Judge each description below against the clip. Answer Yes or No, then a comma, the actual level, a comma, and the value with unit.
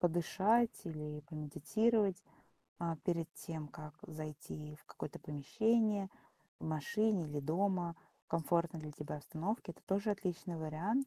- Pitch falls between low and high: Yes, medium, 170 Hz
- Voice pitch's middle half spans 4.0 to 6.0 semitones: Yes, average, 4.7 semitones